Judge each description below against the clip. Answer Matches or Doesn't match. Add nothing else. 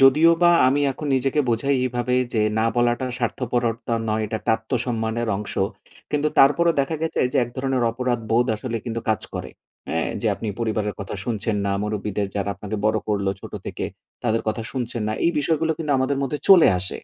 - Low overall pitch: Matches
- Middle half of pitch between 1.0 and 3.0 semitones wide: Doesn't match